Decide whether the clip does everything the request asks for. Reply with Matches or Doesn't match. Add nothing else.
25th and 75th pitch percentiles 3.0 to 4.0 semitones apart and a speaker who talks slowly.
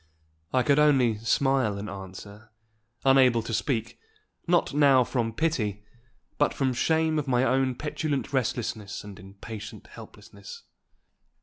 Doesn't match